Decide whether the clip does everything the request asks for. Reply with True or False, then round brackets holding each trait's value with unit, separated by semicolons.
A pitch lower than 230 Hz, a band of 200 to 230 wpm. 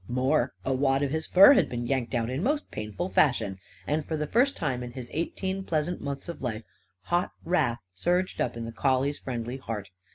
True (135 Hz; 205 wpm)